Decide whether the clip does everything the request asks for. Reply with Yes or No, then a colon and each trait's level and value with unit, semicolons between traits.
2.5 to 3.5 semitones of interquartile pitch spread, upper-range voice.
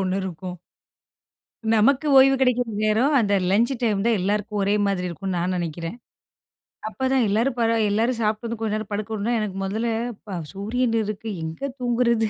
Yes: average, 3.2 semitones; high, 215 Hz